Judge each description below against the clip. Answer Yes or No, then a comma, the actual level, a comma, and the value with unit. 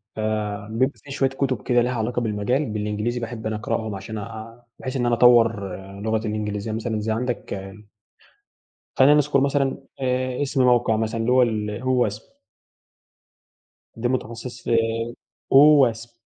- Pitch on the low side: Yes, low, 115 Hz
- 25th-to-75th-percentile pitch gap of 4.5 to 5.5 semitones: No, average, 2.9 semitones